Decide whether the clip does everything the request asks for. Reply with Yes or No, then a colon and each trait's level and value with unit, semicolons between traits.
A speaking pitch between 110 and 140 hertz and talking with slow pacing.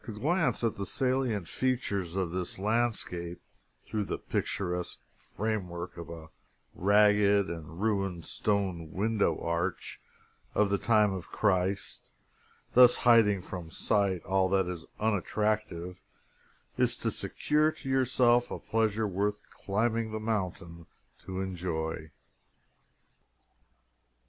No: low, 100 Hz; slow, 115 wpm